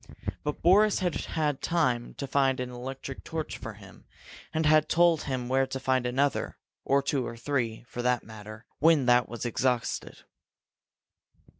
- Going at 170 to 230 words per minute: No, average, 160 wpm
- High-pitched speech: No, low, 135 Hz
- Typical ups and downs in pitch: Yes, average, 3.5 semitones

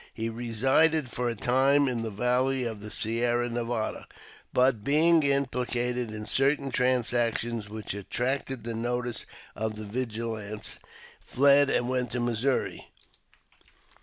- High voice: No, low, 120 Hz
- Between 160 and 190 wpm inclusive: No, slow, 135 wpm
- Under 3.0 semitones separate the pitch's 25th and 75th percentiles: Yes, narrow, 2.6 semitones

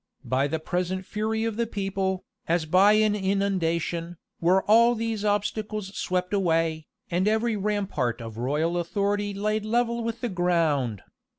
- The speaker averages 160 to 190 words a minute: No, average, 150 wpm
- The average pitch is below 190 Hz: No, high, 195 Hz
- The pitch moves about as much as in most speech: Yes, average, 4.1 semitones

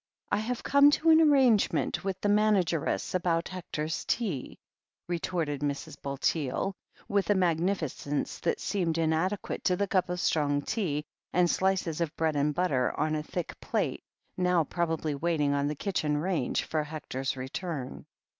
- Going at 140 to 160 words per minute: Yes, average, 155 wpm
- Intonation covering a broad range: No, average, 4.2 semitones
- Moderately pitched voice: Yes, medium, 165 Hz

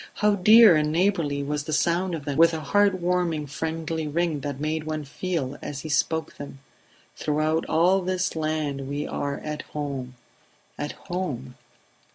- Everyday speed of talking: Yes, average, 165 wpm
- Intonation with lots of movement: No, average, 3.2 semitones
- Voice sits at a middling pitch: Yes, medium, 155 Hz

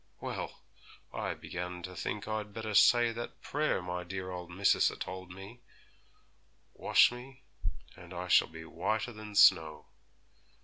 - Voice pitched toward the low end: Yes, very low, 95 Hz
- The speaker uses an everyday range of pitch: Yes, average, 3.6 semitones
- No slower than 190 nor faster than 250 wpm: No, average, 145 wpm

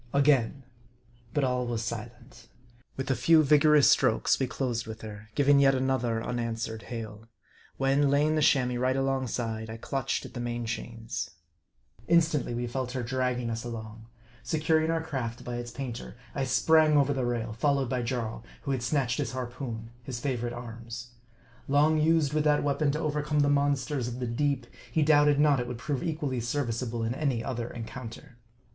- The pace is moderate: Yes, average, 175 wpm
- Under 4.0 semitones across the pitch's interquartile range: Yes, average, 3.5 semitones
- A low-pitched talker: Yes, low, 125 Hz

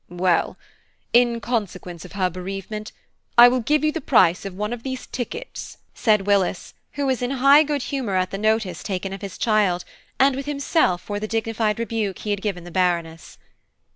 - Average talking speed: Yes, average, 190 wpm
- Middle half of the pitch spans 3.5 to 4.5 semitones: No, average, 4.9 semitones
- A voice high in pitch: Yes, high, 210 Hz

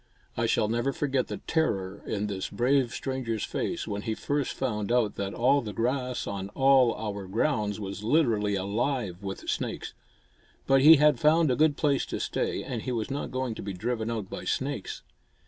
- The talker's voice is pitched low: Yes, low, 120 Hz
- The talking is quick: No, average, 190 wpm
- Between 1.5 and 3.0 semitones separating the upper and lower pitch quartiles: No, average, 4.8 semitones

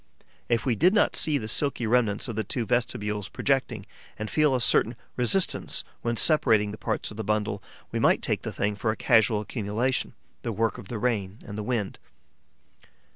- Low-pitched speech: Yes, low, 110 Hz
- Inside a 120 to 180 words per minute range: No, average, 190 wpm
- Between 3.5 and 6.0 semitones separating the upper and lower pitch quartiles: No, average, 3.0 semitones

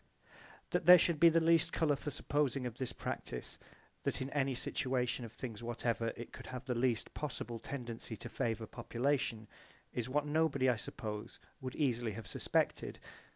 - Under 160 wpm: No, average, 170 wpm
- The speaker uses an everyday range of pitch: Yes, average, 3.9 semitones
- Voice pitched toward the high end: No, low, 125 Hz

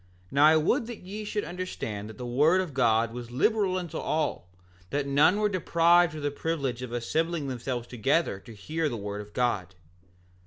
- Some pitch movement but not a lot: No, wide, 6.3 semitones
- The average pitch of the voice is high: No, medium, 145 Hz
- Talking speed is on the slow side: No, average, 195 wpm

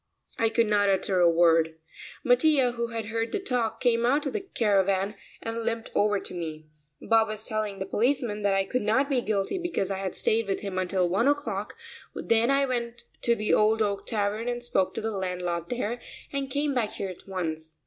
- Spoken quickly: Yes, fast, 210 wpm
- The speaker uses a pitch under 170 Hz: No, high, 215 Hz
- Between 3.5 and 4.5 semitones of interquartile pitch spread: Yes, average, 3.9 semitones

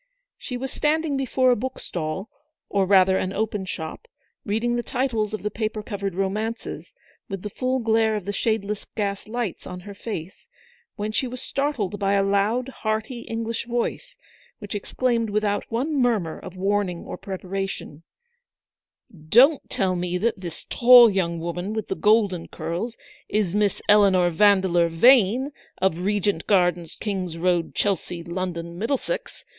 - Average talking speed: Yes, average, 160 wpm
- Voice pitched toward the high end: Yes, high, 205 Hz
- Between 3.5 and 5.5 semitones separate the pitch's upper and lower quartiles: Yes, average, 3.8 semitones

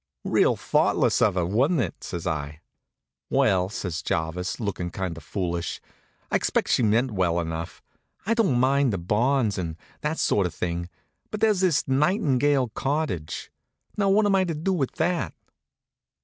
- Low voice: Yes, low, 110 Hz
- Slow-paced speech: No, average, 165 wpm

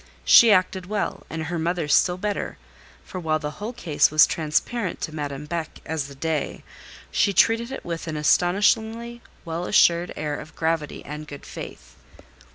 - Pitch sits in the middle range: Yes, medium, 165 Hz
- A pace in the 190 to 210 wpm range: No, average, 165 wpm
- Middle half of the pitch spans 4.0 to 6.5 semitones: Yes, average, 4.5 semitones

